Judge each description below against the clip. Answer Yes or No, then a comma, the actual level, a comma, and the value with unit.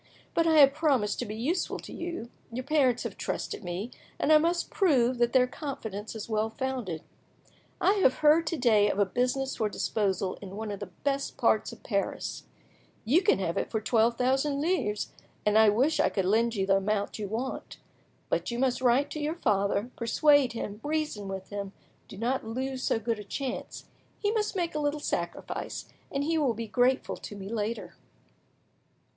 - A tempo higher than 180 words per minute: Yes, average, 195 wpm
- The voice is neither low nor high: No, high, 245 Hz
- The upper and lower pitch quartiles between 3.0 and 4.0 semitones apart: No, wide, 5.4 semitones